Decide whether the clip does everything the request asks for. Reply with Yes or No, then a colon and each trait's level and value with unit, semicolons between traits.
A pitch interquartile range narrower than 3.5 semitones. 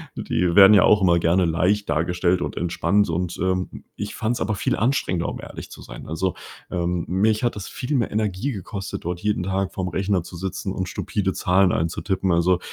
Yes: average, 2.7 semitones